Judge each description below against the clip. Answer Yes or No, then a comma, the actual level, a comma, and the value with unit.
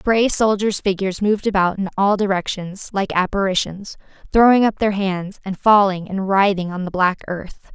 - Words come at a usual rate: Yes, average, 170 wpm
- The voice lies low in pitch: No, high, 195 Hz